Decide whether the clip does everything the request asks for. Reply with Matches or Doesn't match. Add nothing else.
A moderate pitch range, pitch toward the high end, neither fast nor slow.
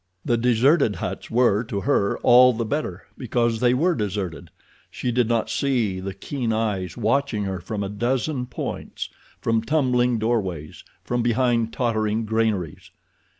Doesn't match